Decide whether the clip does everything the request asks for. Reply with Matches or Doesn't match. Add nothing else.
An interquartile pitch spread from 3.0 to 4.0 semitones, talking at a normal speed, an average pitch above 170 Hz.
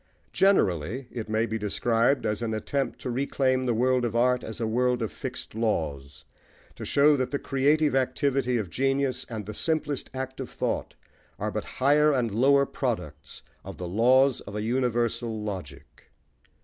Doesn't match